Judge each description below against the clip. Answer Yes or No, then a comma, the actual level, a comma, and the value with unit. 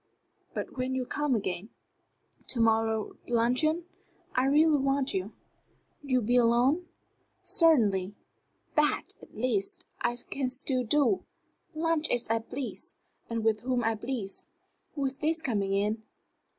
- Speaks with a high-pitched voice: Yes, very high, 250 Hz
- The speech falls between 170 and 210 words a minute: No, slow, 135 wpm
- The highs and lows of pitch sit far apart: No, average, 4.1 semitones